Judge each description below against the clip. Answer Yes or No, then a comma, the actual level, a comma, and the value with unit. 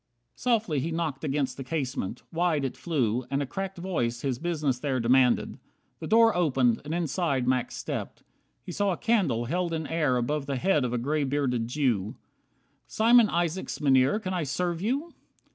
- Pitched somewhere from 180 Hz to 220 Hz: No, medium, 150 Hz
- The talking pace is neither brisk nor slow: Yes, average, 180 wpm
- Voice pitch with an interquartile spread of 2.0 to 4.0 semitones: No, wide, 5.4 semitones